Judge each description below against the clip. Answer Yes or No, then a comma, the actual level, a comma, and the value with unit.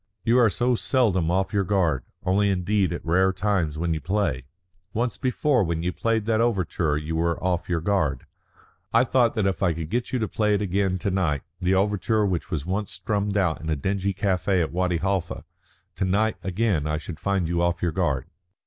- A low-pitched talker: Yes, very low, 95 Hz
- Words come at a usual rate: No, fast, 210 wpm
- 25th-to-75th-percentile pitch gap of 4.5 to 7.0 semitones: No, average, 3.5 semitones